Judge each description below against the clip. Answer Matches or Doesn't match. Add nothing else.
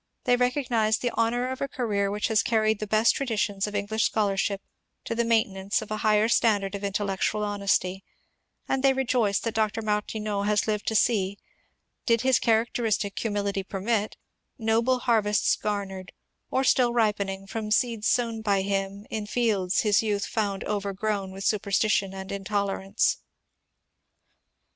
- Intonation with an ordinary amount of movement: Doesn't match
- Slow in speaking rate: Doesn't match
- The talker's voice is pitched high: Matches